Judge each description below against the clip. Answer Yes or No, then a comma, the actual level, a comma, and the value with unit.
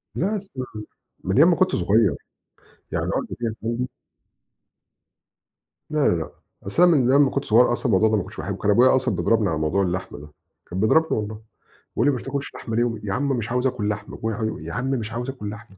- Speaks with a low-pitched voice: Yes, low, 115 Hz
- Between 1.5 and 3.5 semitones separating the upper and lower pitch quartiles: No, average, 4.4 semitones